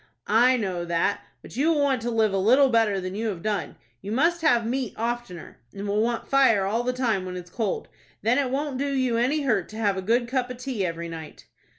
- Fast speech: Yes, fast, 240 wpm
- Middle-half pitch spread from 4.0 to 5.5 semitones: Yes, average, 4.5 semitones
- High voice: Yes, high, 230 Hz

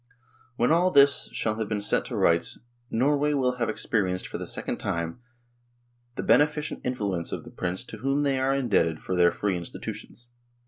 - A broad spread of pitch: Yes, wide, 6.6 semitones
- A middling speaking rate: Yes, average, 185 wpm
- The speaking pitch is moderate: No, low, 120 Hz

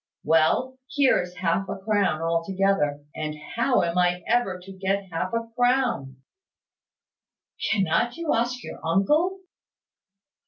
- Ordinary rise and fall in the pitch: No, wide, 6.3 semitones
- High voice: Yes, high, 195 Hz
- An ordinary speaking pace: No, slow, 125 wpm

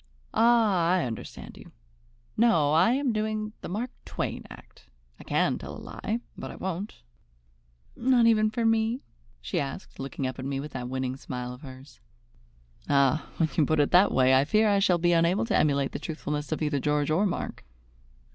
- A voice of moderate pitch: Yes, medium, 165 Hz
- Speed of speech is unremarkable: Yes, average, 190 wpm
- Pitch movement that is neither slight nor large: No, wide, 7.6 semitones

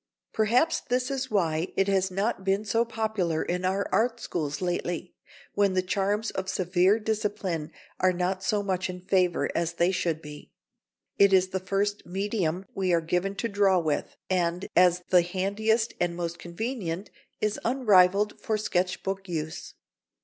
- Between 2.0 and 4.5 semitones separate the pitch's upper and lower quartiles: Yes, average, 2.8 semitones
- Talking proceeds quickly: No, average, 165 wpm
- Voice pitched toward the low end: No, high, 190 Hz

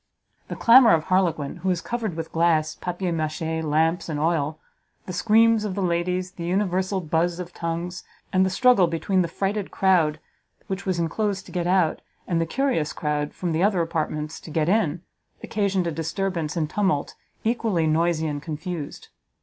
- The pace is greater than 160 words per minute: Yes, average, 175 wpm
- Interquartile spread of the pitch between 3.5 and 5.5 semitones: No, average, 3.0 semitones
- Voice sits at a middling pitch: Yes, medium, 175 Hz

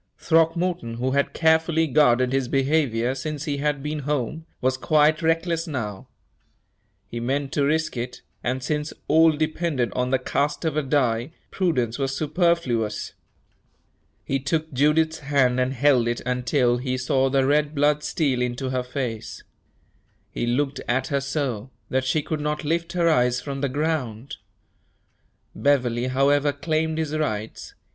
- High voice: No, medium, 140 Hz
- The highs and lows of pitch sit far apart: No, average, 3.5 semitones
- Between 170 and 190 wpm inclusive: No, average, 150 wpm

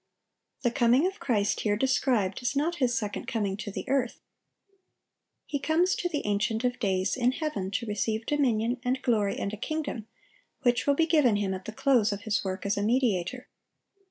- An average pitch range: Yes, average, 4.8 semitones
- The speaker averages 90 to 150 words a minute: No, average, 195 wpm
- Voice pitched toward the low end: No, high, 235 Hz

